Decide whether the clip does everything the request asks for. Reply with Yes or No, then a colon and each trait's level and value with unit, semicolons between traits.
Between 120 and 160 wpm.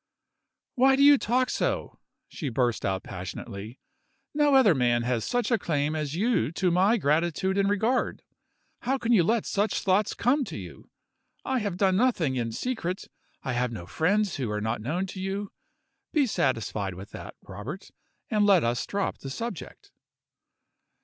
No: average, 170 wpm